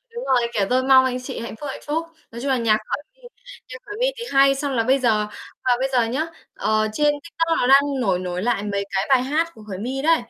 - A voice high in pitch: Yes, very high, 260 Hz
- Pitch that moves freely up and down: No, average, 4.8 semitones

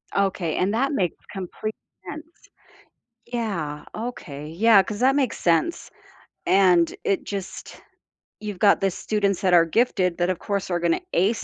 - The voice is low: No, high, 195 Hz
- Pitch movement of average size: Yes, average, 3.9 semitones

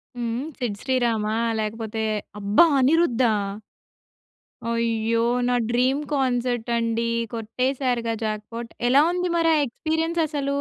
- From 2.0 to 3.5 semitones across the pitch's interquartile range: Yes, average, 2.9 semitones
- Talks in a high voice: Yes, high, 240 Hz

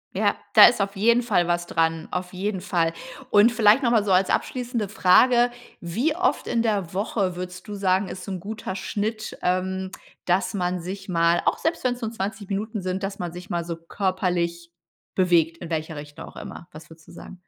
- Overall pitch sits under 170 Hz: No, high, 190 Hz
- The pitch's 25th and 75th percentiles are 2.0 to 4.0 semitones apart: Yes, average, 3.5 semitones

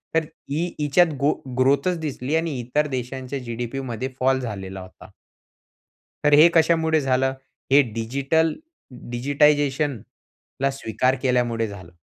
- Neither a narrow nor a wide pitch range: Yes, average, 3.4 semitones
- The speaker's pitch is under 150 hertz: Yes, low, 135 Hz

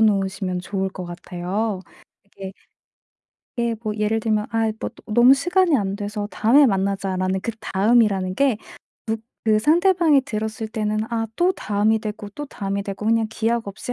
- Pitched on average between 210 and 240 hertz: Yes, high, 215 Hz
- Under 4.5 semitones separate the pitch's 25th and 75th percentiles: Yes, average, 2.8 semitones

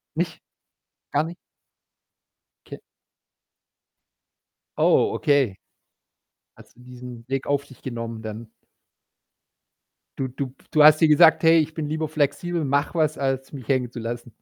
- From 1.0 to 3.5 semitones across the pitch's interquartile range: No, average, 3.9 semitones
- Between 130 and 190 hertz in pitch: Yes, medium, 140 Hz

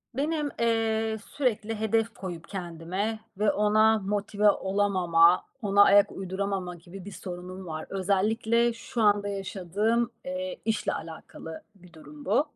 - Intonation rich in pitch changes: No, average, 3.2 semitones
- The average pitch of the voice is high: Yes, high, 205 Hz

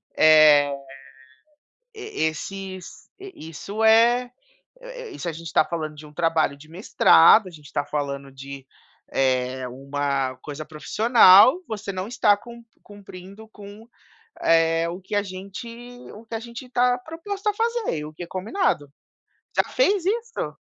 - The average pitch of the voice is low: No, high, 190 Hz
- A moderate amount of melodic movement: No, wide, 7.7 semitones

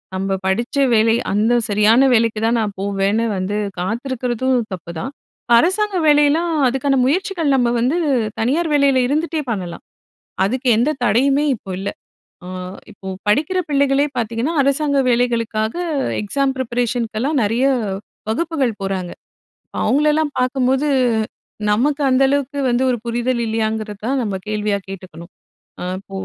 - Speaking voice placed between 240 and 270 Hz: Yes, high, 245 Hz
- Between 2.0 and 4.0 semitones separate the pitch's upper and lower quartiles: No, average, 4.7 semitones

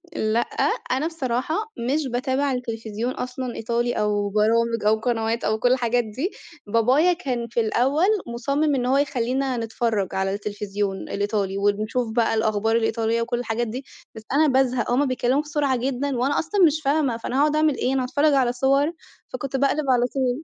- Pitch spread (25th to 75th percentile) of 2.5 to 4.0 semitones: Yes, average, 3.5 semitones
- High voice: Yes, high, 245 Hz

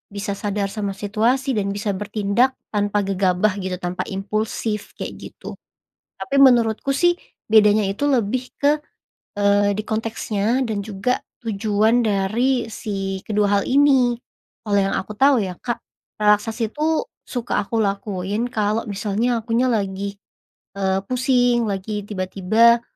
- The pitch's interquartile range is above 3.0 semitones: No, average, 2.7 semitones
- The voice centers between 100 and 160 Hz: No, high, 210 Hz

